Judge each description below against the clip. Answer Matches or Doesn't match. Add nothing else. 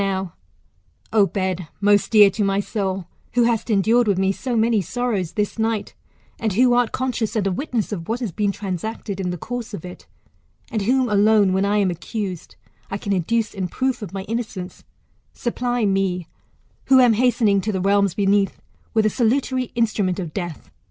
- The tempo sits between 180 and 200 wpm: Matches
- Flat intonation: Doesn't match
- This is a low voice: Doesn't match